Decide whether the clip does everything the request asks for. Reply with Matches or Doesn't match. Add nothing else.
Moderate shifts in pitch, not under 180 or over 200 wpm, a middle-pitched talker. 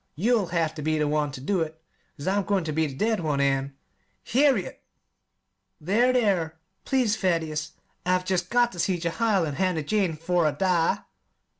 Matches